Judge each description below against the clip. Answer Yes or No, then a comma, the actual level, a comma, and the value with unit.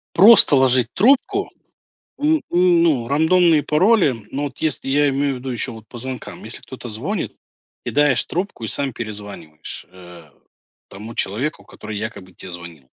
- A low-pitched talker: Yes, low, 130 Hz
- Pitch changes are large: Yes, wide, 7.4 semitones